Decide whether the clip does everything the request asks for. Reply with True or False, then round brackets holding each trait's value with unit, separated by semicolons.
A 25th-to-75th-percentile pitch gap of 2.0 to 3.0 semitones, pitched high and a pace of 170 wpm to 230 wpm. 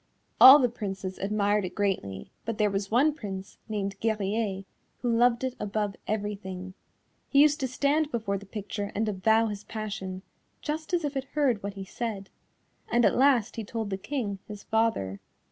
False (3.4 semitones; 210 Hz; 180 wpm)